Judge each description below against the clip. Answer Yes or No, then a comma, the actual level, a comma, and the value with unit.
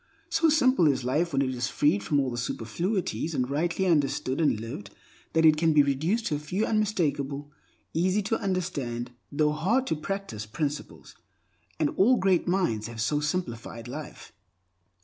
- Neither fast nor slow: Yes, average, 160 wpm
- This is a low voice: No, medium, 150 Hz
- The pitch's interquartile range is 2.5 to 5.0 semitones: No, wide, 5.6 semitones